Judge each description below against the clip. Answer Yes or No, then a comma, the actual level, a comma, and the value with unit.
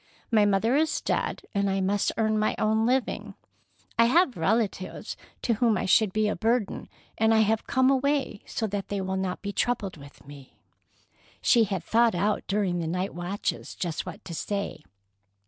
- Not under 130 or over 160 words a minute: No, average, 180 wpm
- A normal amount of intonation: Yes, average, 3.2 semitones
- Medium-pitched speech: No, high, 210 Hz